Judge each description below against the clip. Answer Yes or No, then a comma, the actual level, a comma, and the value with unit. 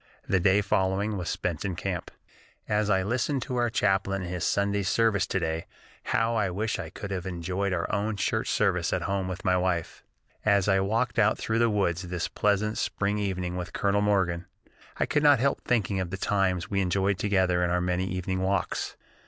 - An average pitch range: No, narrow, 2.2 semitones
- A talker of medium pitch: No, very low, 95 Hz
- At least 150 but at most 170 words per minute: No, average, 200 wpm